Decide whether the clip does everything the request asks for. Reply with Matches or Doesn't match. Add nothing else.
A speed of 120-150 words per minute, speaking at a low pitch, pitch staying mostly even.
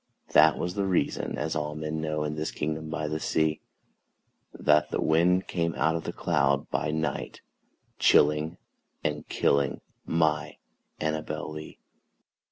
Matches